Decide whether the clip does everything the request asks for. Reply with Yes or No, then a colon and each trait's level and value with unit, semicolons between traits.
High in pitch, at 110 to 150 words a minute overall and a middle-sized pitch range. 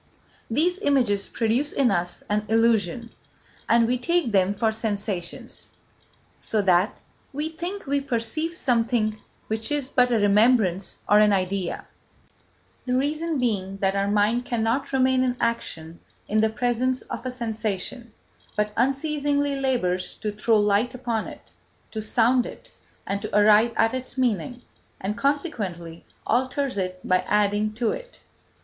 Yes: high, 230 Hz; average, 145 wpm; average, 4.0 semitones